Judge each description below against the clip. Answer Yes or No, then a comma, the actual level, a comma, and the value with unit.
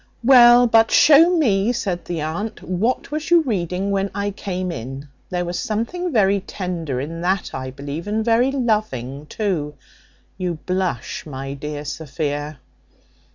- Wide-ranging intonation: Yes, wide, 6.9 semitones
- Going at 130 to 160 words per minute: Yes, average, 150 wpm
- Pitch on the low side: No, medium, 185 Hz